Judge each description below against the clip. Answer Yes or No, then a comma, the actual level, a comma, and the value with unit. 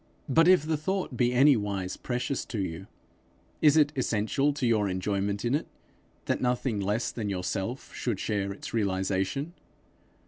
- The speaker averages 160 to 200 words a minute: No, average, 150 wpm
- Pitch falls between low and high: No, low, 115 Hz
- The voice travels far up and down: Yes, wide, 5.9 semitones